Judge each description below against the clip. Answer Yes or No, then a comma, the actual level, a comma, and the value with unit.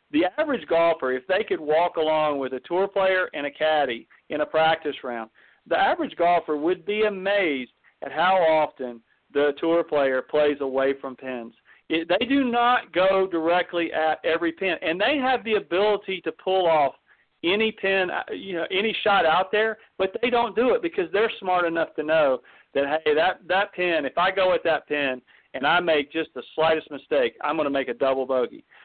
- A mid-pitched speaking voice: Yes, medium, 170 Hz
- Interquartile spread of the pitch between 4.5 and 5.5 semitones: Yes, average, 5.2 semitones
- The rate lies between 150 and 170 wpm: No, average, 200 wpm